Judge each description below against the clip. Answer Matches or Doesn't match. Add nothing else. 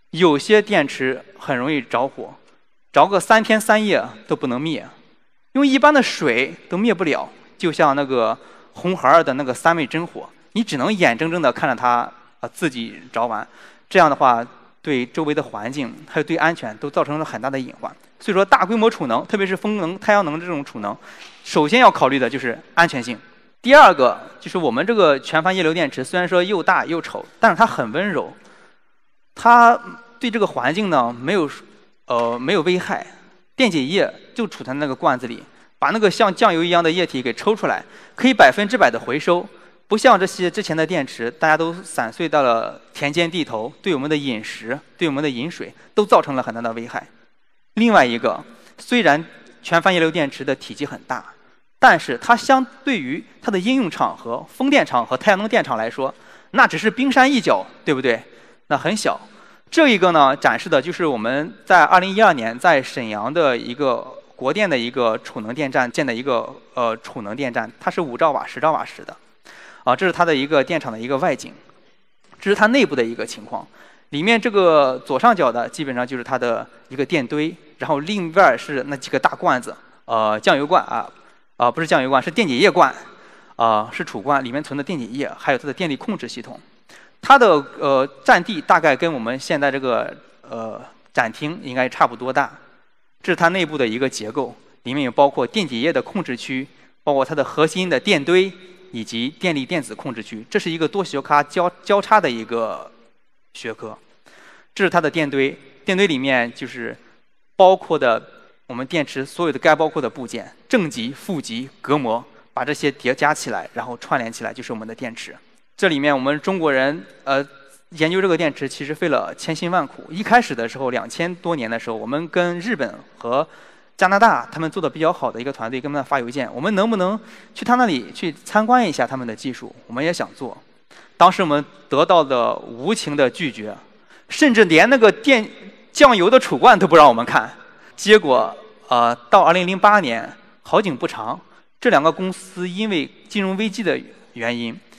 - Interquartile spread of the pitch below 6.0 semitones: Doesn't match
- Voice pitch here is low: Doesn't match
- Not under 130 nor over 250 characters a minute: Doesn't match